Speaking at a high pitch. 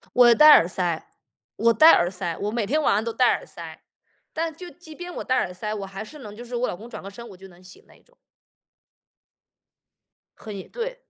Yes: high, 230 Hz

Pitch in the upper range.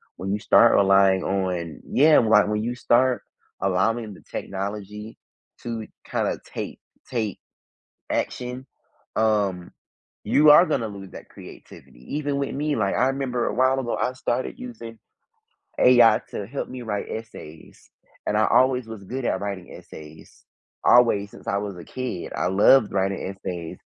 No: low, 110 Hz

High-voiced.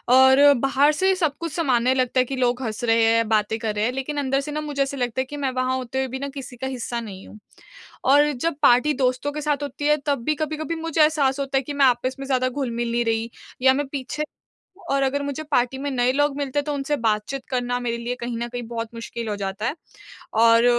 Yes: very high, 265 Hz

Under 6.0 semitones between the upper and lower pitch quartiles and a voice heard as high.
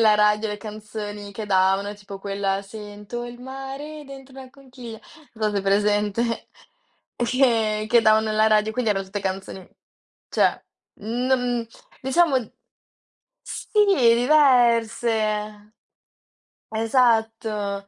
Yes: average, 2.9 semitones; high, 220 Hz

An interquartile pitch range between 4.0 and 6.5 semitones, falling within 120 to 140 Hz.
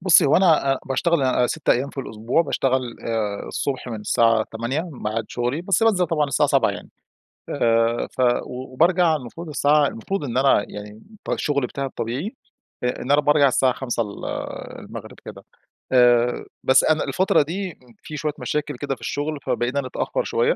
Yes: average, 4.3 semitones; low, 135 Hz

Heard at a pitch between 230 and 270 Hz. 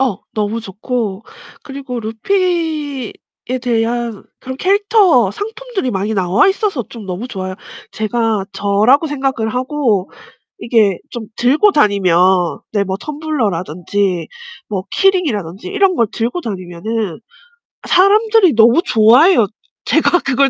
Yes: high, 235 Hz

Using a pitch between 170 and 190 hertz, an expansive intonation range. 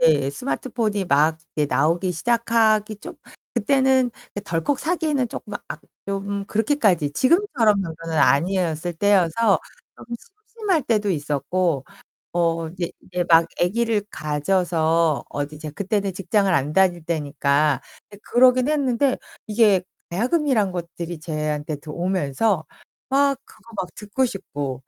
Yes: medium, 185 Hz; wide, 6.3 semitones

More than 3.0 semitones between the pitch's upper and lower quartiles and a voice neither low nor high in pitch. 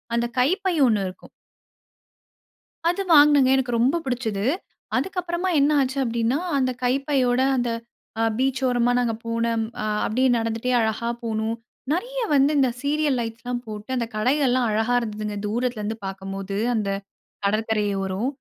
No: average, 3.4 semitones; high, 245 Hz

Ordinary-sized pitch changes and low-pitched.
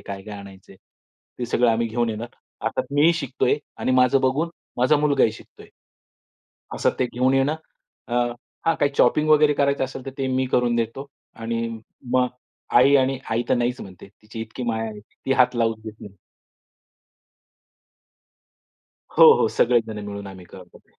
Yes: average, 3.3 semitones; low, 120 Hz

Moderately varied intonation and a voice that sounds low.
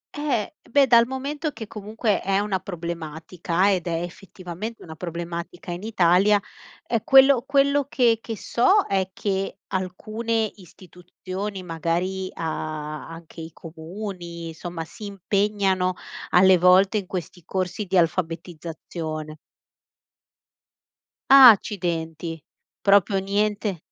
No: average, 3.8 semitones; medium, 185 Hz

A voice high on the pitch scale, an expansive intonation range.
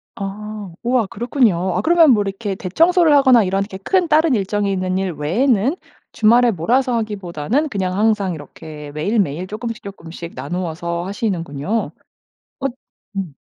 No: high, 200 Hz; average, 4.9 semitones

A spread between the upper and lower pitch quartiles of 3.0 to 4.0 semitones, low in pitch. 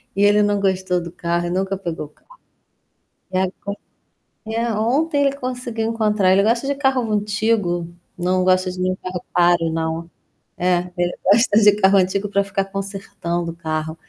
No: average, 3.7 semitones; high, 195 Hz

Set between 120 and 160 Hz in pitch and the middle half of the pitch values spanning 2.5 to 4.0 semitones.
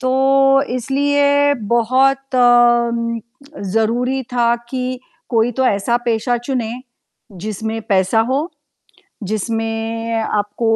No: high, 240 Hz; average, 2.9 semitones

